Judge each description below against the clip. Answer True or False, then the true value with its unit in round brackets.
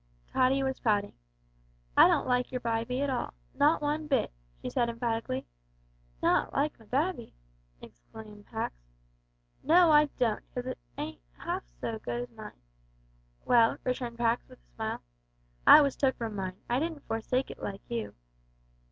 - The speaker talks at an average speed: True (160 wpm)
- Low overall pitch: False (240 Hz)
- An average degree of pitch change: True (3.6 semitones)